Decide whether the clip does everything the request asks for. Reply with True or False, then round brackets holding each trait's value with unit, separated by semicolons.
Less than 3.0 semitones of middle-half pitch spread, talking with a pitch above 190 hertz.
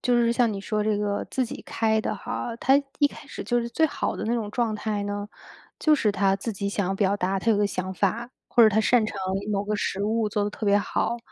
True (2.5 semitones; 210 Hz)